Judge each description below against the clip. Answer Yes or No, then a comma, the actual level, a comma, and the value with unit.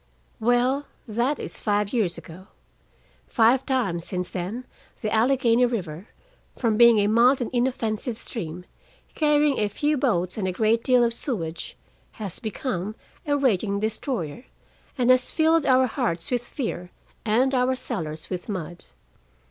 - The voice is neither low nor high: No, high, 230 Hz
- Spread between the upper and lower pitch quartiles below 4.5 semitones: No, average, 4.9 semitones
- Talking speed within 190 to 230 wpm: No, average, 145 wpm